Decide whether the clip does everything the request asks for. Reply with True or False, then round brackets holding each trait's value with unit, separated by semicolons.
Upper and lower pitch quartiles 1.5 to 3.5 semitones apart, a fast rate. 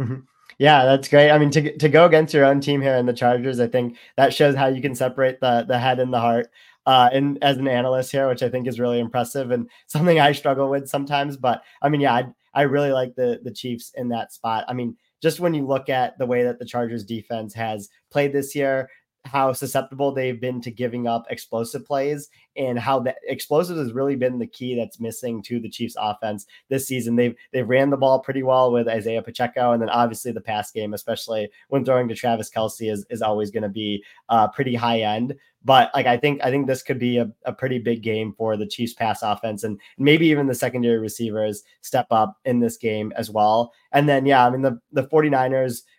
True (2.9 semitones; 230 wpm)